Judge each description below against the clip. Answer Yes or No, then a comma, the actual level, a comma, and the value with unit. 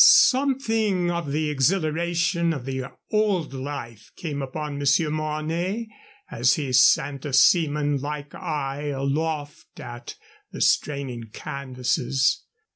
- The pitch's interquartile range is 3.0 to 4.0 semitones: Yes, average, 3.7 semitones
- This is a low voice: No, medium, 150 Hz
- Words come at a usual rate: No, slow, 115 wpm